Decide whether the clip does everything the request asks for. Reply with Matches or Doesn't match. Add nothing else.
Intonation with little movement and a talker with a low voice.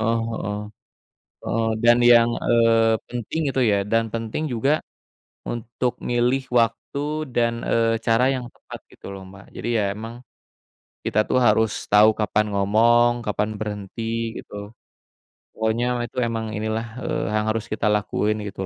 Matches